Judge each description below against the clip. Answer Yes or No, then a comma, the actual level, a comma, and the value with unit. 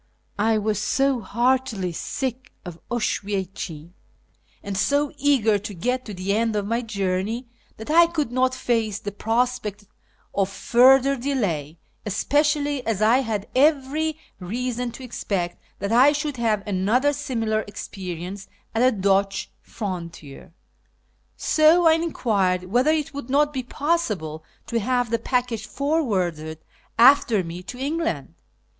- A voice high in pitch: Yes, high, 230 Hz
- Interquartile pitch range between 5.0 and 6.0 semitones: Yes, average, 5.3 semitones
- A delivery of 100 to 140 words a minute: Yes, slow, 135 wpm